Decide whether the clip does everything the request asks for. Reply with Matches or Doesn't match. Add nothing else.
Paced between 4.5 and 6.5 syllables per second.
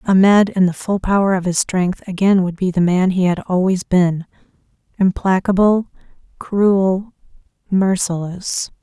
Doesn't match